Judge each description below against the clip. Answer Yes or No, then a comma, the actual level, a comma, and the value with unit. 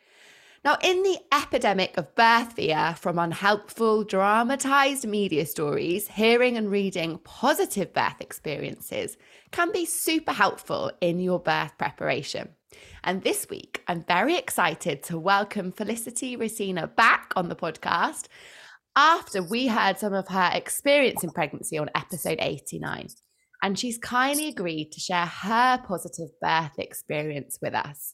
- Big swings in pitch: Yes, wide, 7.4 semitones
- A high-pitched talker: Yes, high, 210 Hz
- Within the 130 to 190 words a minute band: Yes, slow, 135 wpm